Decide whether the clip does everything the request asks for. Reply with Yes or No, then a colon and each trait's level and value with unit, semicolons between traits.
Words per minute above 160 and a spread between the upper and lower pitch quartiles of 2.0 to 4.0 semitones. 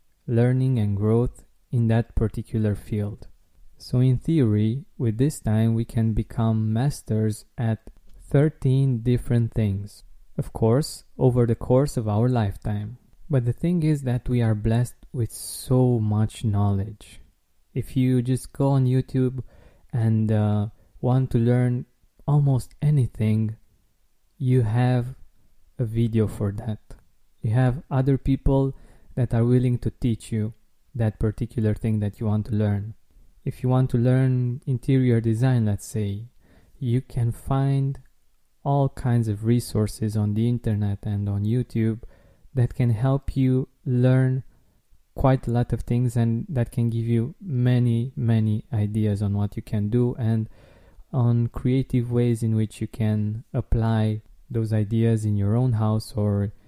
No: average, 145 wpm; average, 2.8 semitones